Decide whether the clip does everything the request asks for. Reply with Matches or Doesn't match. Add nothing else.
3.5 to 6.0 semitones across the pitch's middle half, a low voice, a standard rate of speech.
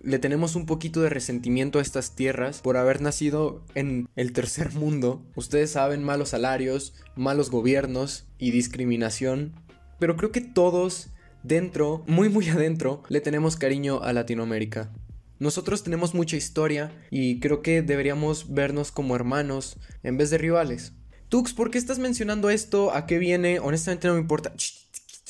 Doesn't match